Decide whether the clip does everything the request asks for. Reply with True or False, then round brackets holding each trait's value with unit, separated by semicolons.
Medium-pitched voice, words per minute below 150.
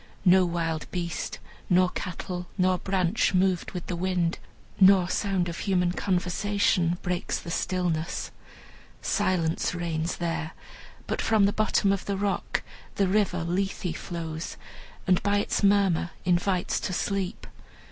True (180 Hz; 135 wpm)